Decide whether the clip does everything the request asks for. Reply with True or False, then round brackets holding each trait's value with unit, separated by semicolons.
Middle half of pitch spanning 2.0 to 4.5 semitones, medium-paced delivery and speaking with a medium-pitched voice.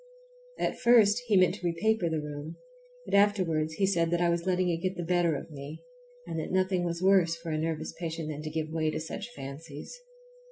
False (3.0 semitones; 215 wpm; 170 Hz)